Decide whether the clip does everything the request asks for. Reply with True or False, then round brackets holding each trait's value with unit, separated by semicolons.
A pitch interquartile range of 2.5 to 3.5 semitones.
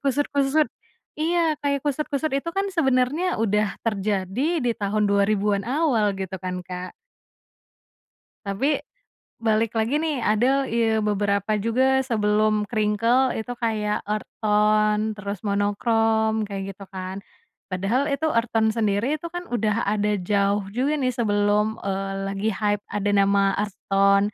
False (3.9 semitones)